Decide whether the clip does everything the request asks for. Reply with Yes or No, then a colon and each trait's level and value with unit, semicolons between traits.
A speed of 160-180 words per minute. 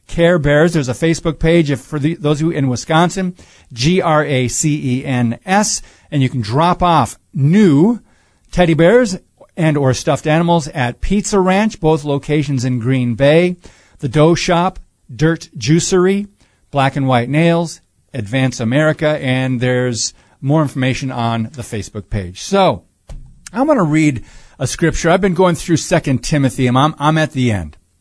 Yes: average, 165 wpm